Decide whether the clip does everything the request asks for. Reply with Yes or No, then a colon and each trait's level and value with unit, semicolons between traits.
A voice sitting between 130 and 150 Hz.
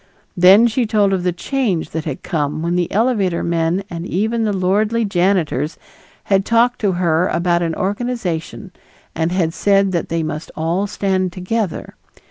No: medium, 185 Hz